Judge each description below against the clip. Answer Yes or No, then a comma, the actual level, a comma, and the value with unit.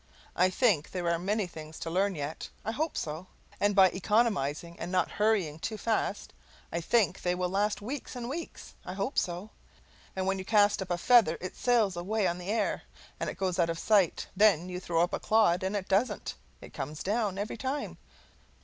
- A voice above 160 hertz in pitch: Yes, high, 190 Hz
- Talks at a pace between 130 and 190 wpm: No, average, 200 wpm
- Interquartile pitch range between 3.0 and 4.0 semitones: Yes, average, 3.7 semitones